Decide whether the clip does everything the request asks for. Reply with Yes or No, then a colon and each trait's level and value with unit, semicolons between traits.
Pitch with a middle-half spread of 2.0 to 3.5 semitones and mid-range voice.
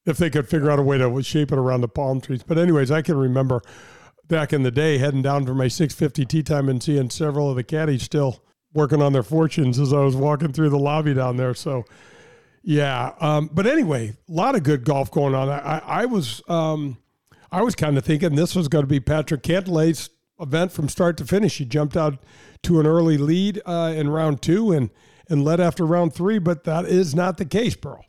Yes: average, 3.1 semitones; medium, 150 Hz